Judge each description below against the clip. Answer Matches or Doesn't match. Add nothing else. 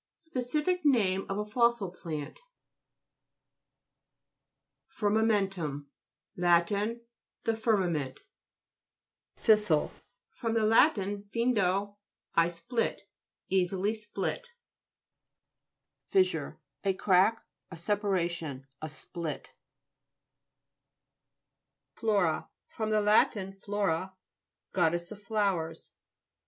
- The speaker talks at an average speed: Doesn't match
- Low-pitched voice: Doesn't match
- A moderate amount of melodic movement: Matches